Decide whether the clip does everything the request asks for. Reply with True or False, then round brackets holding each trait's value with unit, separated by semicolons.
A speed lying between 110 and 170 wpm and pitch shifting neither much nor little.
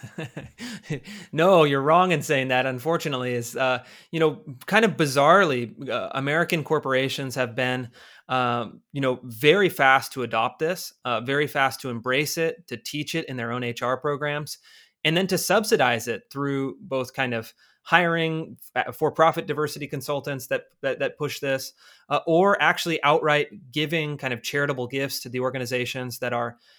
True (165 wpm; 4.0 semitones)